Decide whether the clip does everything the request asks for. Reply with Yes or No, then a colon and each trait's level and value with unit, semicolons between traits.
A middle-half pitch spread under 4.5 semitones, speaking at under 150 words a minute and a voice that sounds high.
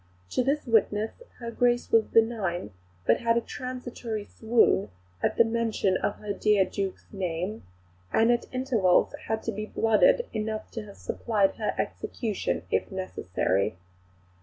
Yes: average, 2.9 semitones; average, 140 wpm; high, 220 Hz